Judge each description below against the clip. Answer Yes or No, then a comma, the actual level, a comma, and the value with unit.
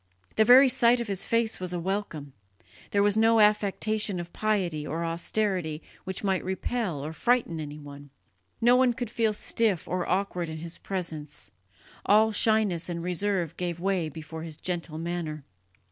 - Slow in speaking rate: No, average, 160 wpm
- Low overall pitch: No, medium, 185 Hz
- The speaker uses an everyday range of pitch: Yes, average, 4.7 semitones